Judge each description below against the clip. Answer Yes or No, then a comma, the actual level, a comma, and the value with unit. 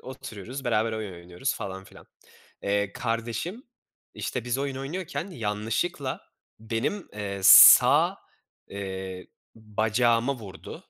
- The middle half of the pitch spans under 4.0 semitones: No, average, 4.7 semitones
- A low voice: Yes, low, 115 Hz